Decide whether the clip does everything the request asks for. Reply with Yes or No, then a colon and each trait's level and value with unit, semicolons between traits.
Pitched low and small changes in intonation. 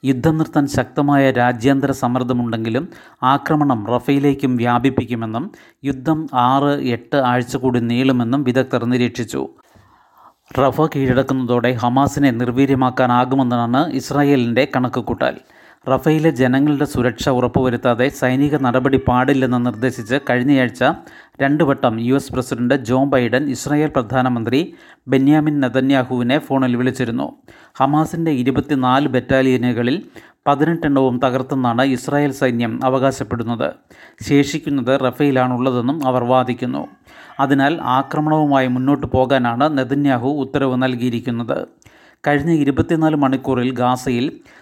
Yes: low, 130 Hz; narrow, 2.1 semitones